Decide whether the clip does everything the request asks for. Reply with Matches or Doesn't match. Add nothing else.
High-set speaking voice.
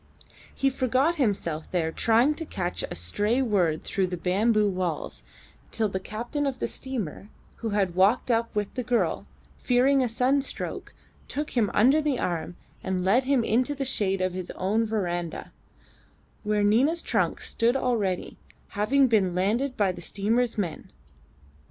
Matches